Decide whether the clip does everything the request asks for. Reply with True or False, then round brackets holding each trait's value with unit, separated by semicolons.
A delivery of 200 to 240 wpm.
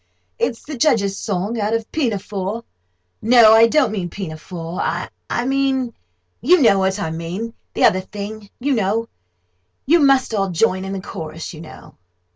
False (140 wpm)